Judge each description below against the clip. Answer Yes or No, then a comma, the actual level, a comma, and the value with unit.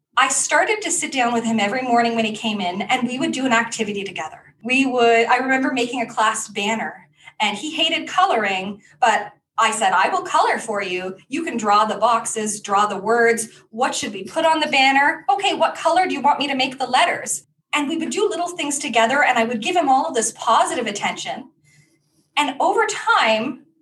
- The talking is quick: Yes, fast, 215 wpm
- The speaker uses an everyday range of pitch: No, wide, 5.8 semitones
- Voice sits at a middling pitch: No, high, 240 Hz